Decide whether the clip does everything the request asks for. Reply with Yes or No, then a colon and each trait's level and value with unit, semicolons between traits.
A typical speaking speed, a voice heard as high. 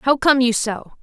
No: fast, 235 wpm; very high, 250 Hz